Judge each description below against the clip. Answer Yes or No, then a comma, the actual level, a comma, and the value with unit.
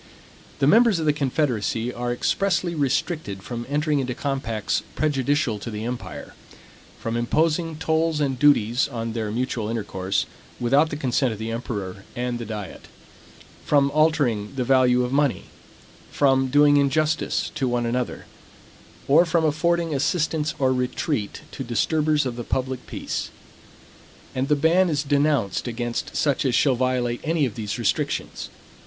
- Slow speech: No, average, 150 wpm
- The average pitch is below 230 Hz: Yes, low, 135 Hz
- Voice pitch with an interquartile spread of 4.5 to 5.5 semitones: No, average, 4.1 semitones